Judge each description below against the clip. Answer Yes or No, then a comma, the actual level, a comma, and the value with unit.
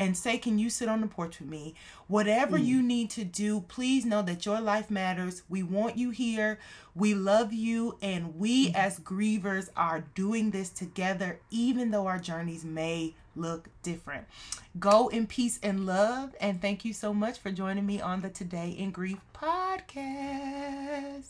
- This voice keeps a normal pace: Yes, average, 175 wpm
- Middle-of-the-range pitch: No, high, 205 Hz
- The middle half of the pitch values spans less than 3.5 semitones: No, average, 3.8 semitones